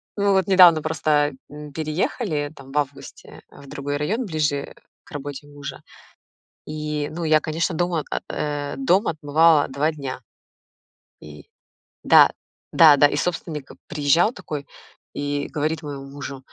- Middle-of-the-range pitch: Yes, medium, 150 Hz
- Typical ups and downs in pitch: No, narrow, 2.1 semitones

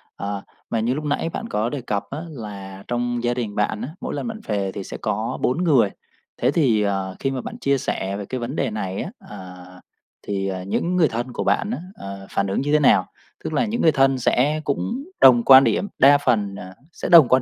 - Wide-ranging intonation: Yes, wide, 6.1 semitones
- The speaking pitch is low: Yes, low, 120 Hz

